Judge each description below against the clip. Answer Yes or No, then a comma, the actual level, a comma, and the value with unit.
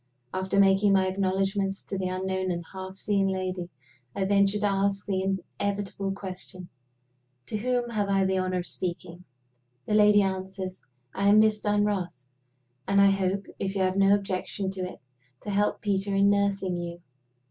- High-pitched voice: Yes, high, 195 Hz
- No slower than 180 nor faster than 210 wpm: No, average, 170 wpm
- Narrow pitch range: Yes, narrow, 1.2 semitones